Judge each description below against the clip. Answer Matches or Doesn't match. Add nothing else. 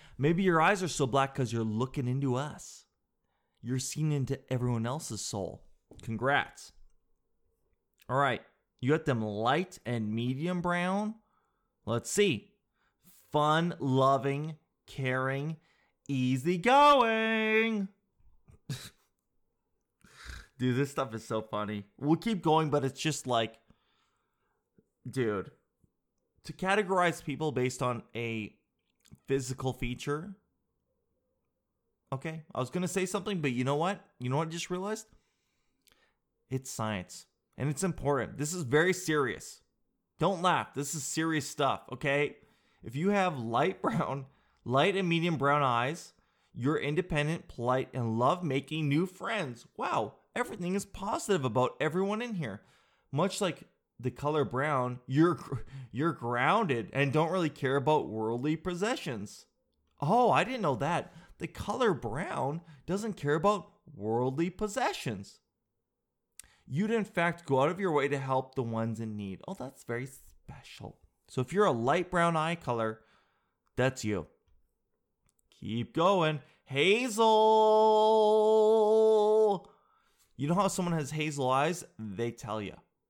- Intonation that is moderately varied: Doesn't match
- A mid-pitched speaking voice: Matches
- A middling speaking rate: Doesn't match